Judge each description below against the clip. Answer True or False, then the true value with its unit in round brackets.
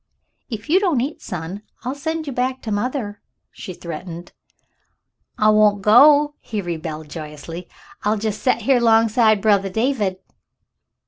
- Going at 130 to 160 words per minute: True (140 wpm)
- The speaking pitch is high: True (215 Hz)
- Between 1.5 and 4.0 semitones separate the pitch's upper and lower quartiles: False (5.3 semitones)